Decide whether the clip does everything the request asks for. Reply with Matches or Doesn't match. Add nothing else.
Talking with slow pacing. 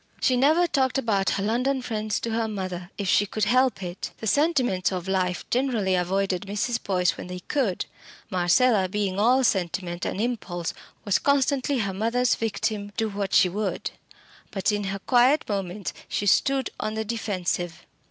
Doesn't match